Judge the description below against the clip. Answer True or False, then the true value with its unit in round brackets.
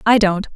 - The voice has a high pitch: True (205 Hz)